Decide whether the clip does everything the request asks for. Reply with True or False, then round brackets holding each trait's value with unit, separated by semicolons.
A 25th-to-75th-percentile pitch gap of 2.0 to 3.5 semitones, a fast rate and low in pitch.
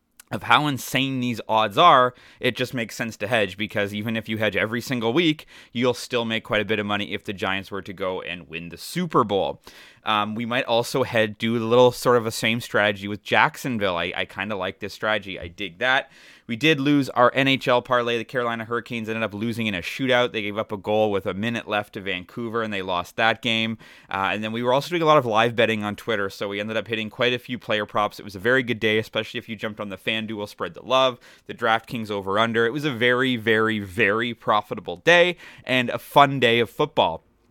True (2.8 semitones; 245 wpm; 115 Hz)